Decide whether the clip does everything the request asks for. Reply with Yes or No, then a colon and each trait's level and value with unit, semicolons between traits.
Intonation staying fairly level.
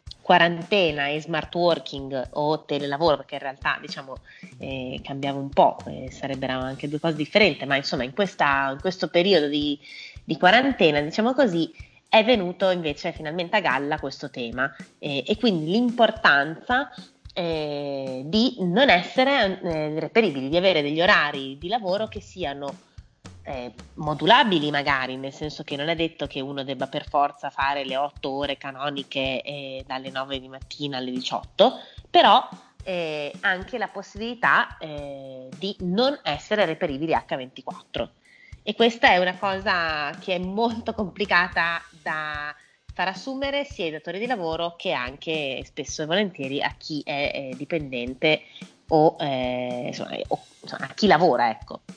No: average, 5.0 semitones